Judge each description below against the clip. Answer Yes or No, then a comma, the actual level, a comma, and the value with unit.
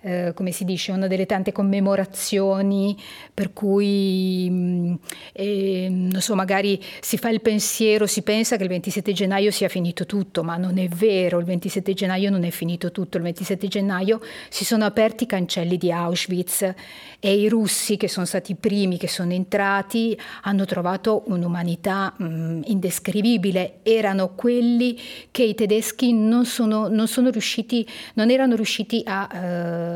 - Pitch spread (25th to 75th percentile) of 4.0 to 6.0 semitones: No, average, 2.8 semitones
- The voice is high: Yes, high, 195 Hz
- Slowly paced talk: No, average, 160 wpm